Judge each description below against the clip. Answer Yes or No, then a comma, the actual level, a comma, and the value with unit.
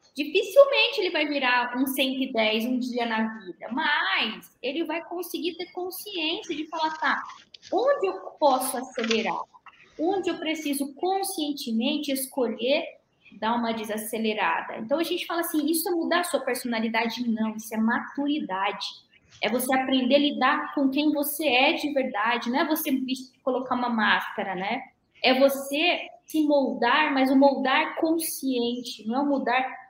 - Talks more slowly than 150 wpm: No, average, 155 wpm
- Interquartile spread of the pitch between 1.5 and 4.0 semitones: No, average, 4.4 semitones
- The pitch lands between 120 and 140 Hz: No, very high, 275 Hz